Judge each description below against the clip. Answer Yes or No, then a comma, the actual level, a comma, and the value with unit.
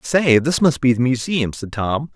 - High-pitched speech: No, low, 130 Hz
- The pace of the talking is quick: Yes, fast, 225 wpm